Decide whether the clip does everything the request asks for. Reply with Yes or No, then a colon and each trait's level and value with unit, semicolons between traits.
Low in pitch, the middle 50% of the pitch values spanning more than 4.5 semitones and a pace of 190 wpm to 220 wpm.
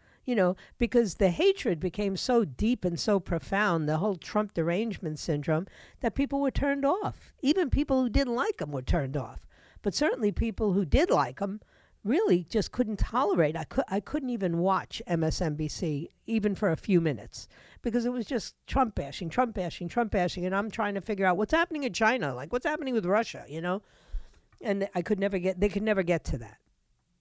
No: high, 205 Hz; average, 5.3 semitones; average, 200 wpm